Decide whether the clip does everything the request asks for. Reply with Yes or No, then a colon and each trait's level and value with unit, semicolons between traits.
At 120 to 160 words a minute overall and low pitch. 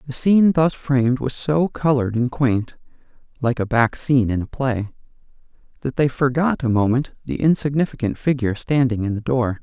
No: average, 175 wpm; low, 130 Hz